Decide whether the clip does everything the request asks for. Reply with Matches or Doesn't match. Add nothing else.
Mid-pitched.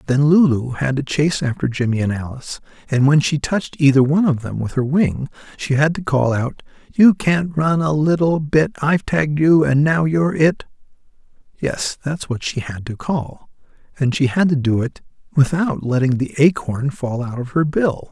Matches